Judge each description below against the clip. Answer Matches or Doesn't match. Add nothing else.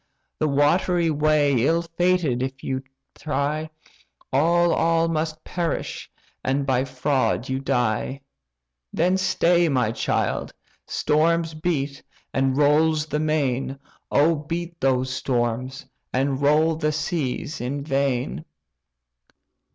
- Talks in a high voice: Doesn't match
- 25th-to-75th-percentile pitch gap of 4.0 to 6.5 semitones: Doesn't match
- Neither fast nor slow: Doesn't match